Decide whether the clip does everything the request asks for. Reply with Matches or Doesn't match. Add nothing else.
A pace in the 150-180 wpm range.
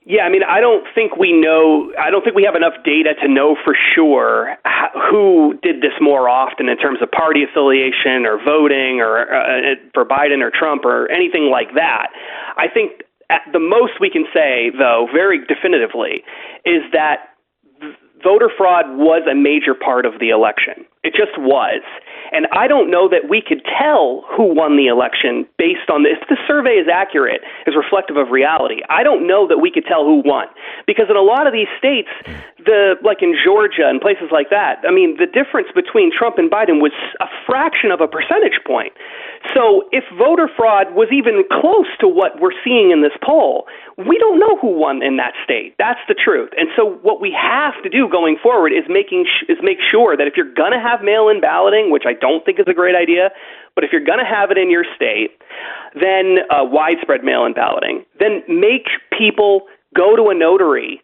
Doesn't match